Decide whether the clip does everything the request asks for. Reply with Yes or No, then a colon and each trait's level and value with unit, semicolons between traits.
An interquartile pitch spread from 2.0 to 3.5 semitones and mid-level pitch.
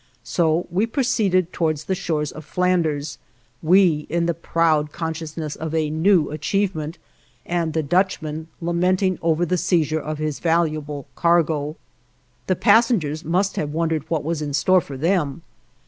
Yes: average, 2.7 semitones; medium, 165 Hz